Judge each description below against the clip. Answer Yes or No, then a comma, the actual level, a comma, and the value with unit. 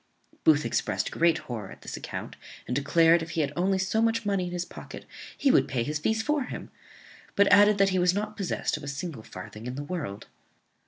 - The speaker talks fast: Yes, fast, 220 wpm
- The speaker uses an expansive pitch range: Yes, wide, 6.2 semitones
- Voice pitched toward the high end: No, medium, 170 Hz